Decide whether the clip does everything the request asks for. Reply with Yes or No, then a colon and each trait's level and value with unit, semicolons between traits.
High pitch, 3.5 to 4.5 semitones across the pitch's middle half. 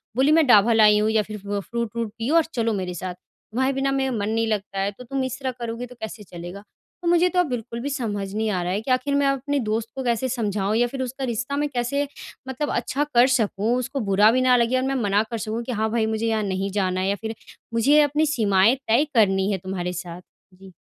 Yes: high, 230 Hz; average, 4.2 semitones